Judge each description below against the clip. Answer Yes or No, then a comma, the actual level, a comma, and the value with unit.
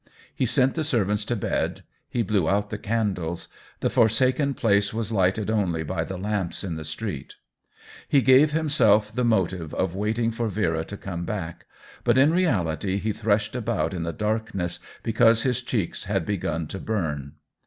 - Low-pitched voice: Yes, low, 105 Hz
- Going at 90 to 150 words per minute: No, average, 175 wpm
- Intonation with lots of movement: No, average, 4.4 semitones